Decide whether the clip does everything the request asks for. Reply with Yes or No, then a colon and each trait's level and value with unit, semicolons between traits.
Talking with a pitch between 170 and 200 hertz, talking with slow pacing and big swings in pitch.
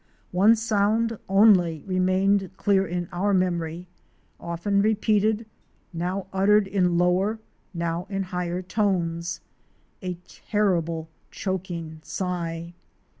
No: medium, 185 Hz; slow, 105 wpm; average, 2.8 semitones